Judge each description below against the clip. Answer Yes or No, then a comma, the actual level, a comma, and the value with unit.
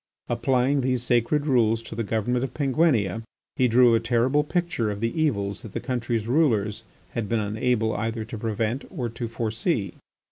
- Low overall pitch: Yes, low, 115 Hz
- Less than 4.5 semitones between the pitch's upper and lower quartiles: Yes, average, 2.7 semitones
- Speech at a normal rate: Yes, average, 175 wpm